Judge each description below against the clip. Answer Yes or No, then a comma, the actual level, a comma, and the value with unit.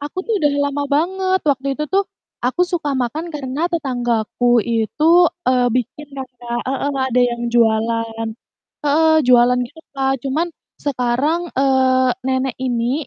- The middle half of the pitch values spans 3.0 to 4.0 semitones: Yes, average, 3.7 semitones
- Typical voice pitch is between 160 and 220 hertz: No, very high, 265 Hz